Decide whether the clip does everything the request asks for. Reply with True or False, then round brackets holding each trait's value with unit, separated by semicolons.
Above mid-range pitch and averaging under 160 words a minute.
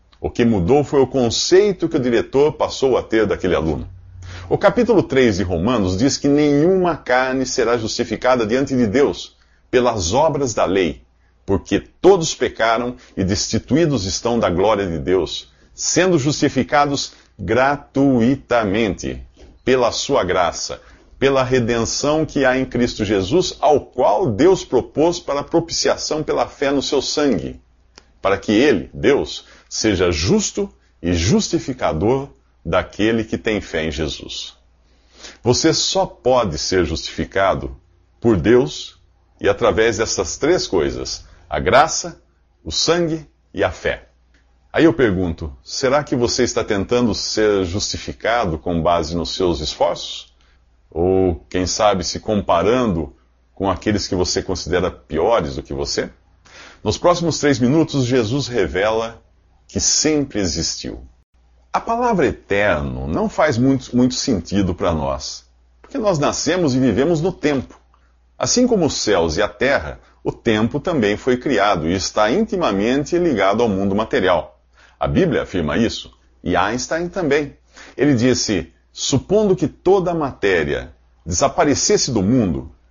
False (115 Hz; 140 wpm)